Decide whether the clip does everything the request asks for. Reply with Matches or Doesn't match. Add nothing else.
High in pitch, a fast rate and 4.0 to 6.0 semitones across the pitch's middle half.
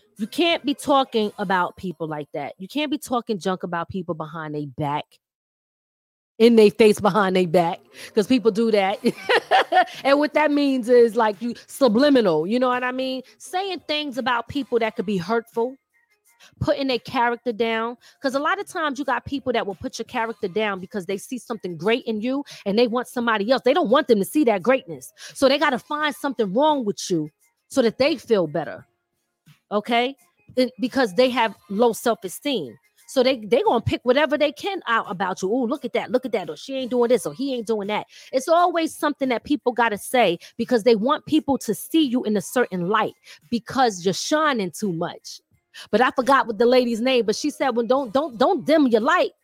Matches